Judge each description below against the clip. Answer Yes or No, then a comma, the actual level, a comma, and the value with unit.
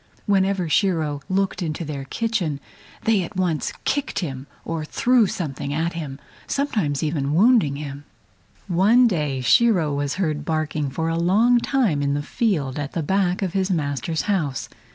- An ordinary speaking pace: Yes, average, 170 wpm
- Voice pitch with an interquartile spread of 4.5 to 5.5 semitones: Yes, average, 5.2 semitones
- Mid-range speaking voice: Yes, medium, 165 Hz